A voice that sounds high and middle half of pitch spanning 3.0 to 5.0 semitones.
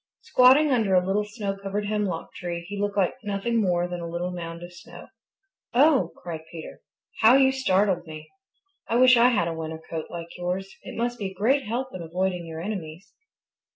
Yes: high, 195 Hz; average, 4.6 semitones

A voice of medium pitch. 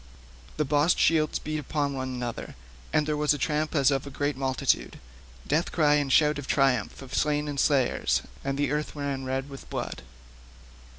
Yes: medium, 145 Hz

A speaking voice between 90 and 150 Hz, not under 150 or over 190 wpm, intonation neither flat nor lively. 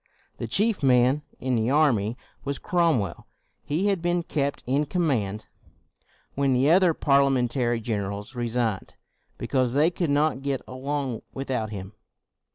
No: low, 135 Hz; slow, 135 wpm; average, 4.1 semitones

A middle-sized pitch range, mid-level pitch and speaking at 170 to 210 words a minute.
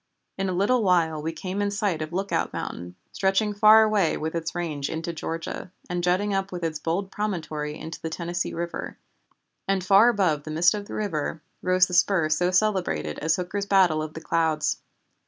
Yes: average, 3.5 semitones; medium, 175 Hz; average, 190 wpm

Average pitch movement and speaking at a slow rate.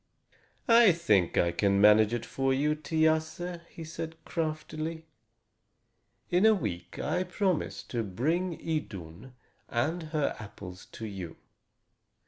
No: wide, 7.9 semitones; slow, 120 wpm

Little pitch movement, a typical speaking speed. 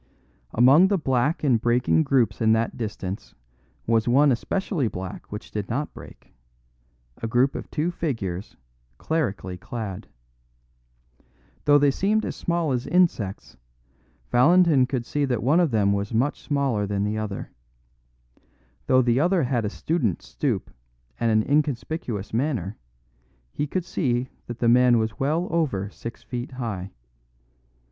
No: average, 5.2 semitones; average, 145 wpm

